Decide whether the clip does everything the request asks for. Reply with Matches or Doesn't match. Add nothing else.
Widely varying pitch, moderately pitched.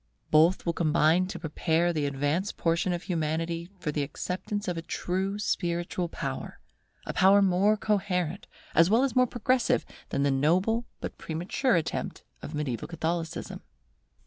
Doesn't match